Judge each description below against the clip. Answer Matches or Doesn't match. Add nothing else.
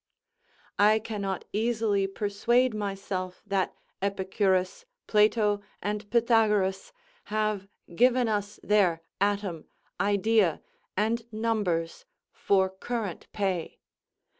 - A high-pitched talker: Matches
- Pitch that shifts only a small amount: Matches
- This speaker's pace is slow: Matches